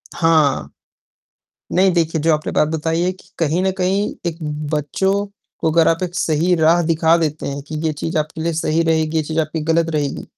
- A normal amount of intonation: No, narrow, 1.6 semitones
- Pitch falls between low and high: Yes, medium, 160 Hz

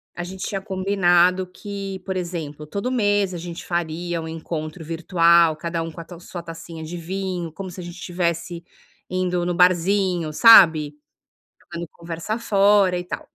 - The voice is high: No, medium, 175 Hz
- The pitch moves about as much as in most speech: No, narrow, 2.2 semitones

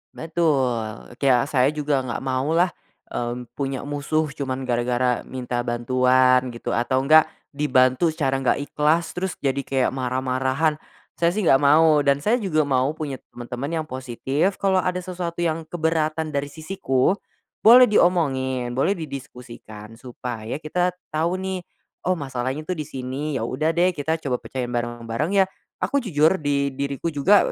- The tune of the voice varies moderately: Yes, average, 4.0 semitones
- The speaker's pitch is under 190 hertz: Yes, medium, 140 Hz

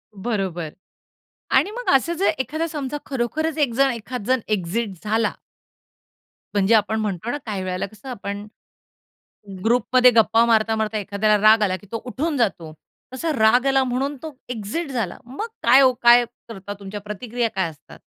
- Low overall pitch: No, high, 230 Hz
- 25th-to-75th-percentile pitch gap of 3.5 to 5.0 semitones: Yes, average, 4.1 semitones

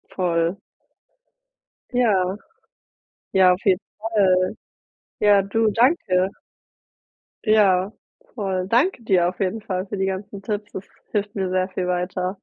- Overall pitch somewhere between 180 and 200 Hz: Yes, high, 190 Hz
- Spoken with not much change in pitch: Yes, narrow, 2.3 semitones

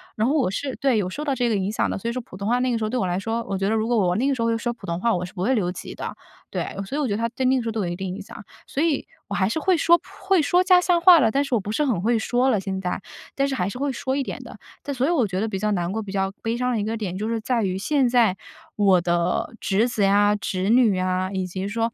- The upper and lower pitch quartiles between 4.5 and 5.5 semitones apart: Yes, average, 4.9 semitones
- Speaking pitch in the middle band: No, high, 225 Hz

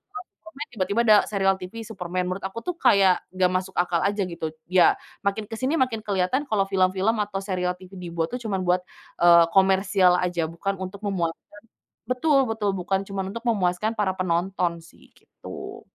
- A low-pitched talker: No, high, 190 Hz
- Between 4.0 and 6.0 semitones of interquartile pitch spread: No, average, 2.8 semitones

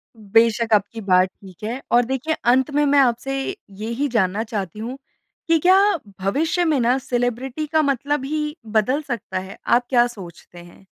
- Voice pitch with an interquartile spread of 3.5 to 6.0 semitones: Yes, average, 4.6 semitones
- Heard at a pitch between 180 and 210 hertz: No, high, 240 Hz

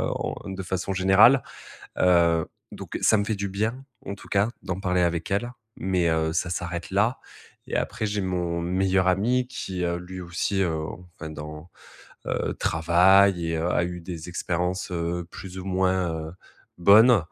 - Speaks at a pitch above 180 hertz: No, very low, 90 Hz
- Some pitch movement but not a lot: No, narrow, 2.2 semitones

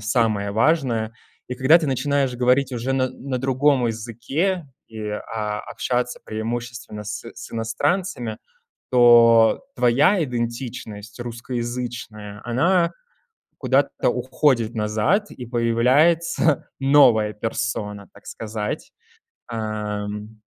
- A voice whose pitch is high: No, low, 120 Hz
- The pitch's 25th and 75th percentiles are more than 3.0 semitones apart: Yes, average, 3.5 semitones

